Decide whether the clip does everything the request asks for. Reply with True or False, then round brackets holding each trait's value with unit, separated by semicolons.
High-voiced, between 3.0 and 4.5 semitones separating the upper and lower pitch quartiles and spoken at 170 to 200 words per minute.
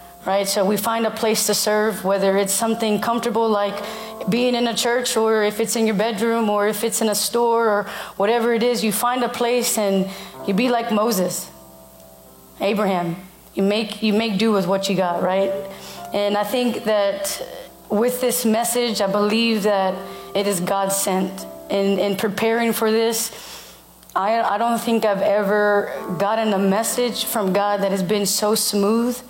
False (210 Hz; 2.5 semitones; 180 wpm)